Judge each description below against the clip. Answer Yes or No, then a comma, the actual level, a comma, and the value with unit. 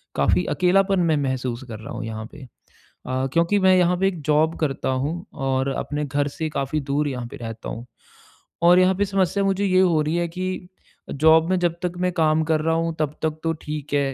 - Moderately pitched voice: Yes, medium, 160 Hz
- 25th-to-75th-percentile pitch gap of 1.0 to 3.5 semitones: No, average, 4.5 semitones